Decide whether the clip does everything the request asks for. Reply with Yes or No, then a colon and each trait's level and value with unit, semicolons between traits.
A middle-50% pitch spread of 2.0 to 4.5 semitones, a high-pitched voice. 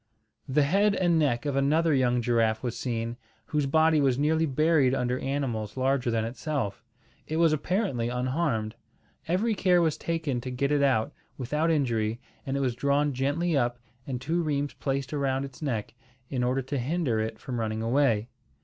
No: average, 3.9 semitones; low, 135 Hz